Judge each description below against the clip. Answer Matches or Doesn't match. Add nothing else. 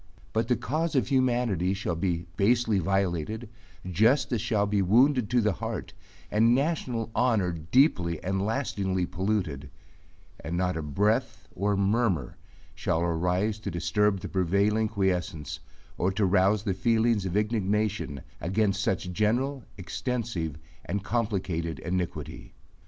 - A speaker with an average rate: Doesn't match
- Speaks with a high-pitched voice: Doesn't match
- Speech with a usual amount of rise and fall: Matches